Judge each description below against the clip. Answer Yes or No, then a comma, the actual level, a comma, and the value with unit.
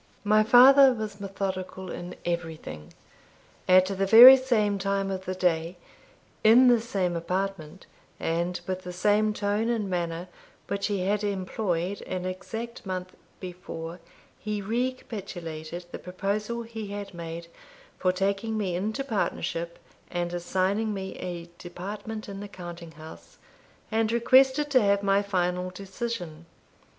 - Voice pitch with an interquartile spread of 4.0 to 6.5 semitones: No, average, 3.3 semitones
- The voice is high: Yes, high, 195 Hz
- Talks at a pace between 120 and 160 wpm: Yes, slow, 135 wpm